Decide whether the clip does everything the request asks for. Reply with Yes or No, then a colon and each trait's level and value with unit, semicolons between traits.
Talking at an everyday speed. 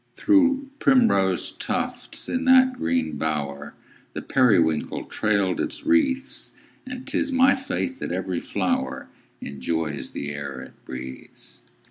No: slow, 120 wpm